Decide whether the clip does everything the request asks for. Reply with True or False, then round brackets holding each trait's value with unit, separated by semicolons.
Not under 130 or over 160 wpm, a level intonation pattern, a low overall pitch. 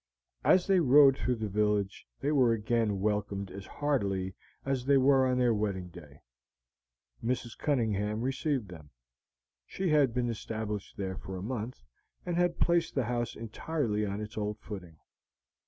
False (155 wpm; 4.8 semitones; 115 Hz)